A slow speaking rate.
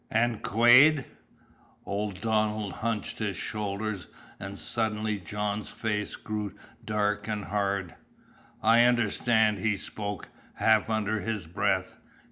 Yes: slow, 110 wpm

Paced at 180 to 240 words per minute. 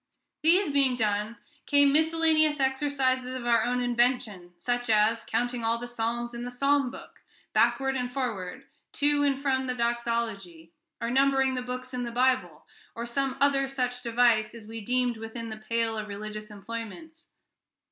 No: average, 165 wpm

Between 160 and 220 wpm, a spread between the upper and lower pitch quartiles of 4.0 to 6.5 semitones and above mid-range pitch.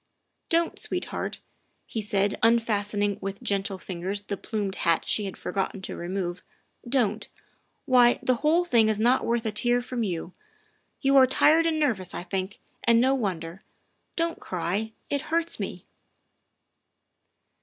Yes: average, 170 wpm; average, 4.5 semitones; high, 215 Hz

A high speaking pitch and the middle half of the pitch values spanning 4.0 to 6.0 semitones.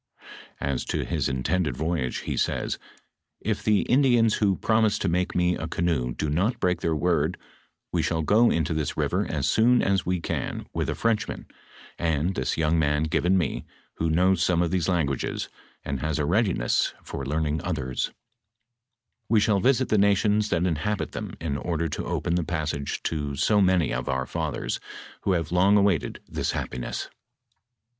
No: very low, 85 Hz; average, 4.3 semitones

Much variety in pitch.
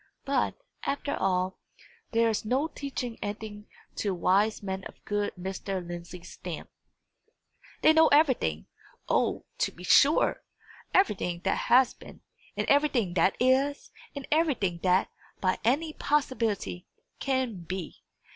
Yes: wide, 6.8 semitones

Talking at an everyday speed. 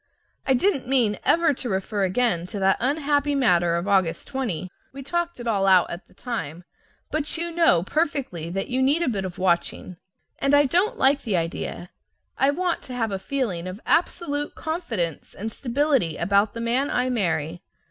Yes: average, 185 wpm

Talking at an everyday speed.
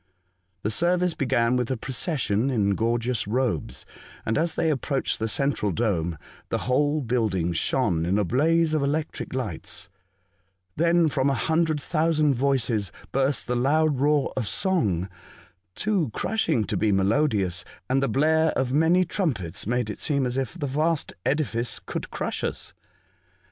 Yes: average, 155 wpm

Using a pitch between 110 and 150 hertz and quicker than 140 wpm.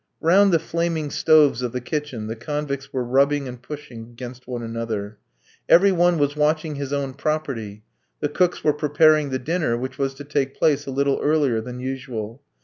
Yes: medium, 140 Hz; average, 185 wpm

